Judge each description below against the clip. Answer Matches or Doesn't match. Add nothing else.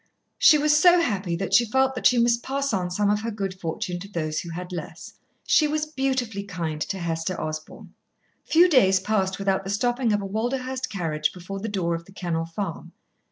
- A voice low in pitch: Doesn't match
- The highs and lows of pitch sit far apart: Matches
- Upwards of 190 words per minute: Matches